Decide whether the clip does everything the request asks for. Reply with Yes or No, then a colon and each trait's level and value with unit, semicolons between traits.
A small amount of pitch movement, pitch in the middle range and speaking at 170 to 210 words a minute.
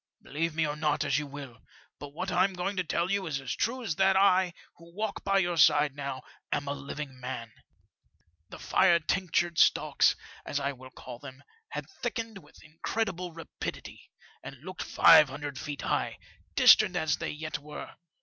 No: average, 4.5 semitones; medium, 155 Hz; average, 185 wpm